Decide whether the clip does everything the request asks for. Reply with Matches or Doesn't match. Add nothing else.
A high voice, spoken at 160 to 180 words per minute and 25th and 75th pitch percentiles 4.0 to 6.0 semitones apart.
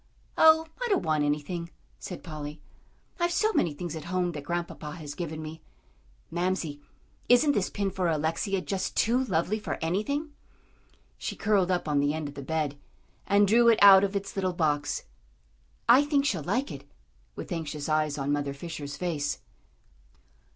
Doesn't match